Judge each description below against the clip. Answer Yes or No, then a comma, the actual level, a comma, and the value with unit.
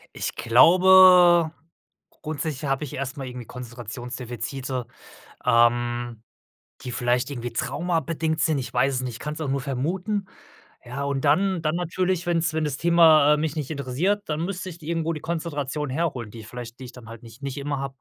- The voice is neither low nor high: Yes, medium, 145 Hz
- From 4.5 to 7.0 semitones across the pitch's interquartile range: Yes, average, 4.8 semitones